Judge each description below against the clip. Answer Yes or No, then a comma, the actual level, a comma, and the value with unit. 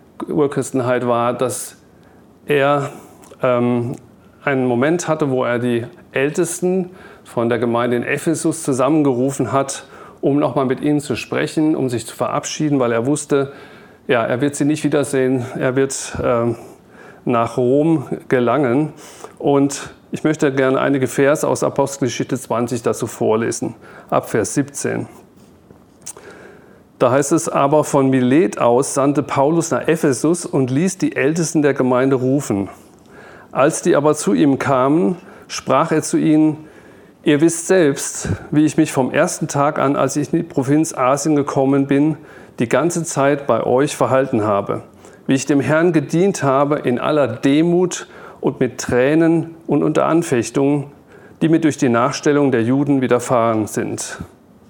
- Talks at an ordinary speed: Yes, average, 150 wpm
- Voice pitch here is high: No, medium, 140 Hz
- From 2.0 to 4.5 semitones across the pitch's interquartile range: Yes, average, 3.0 semitones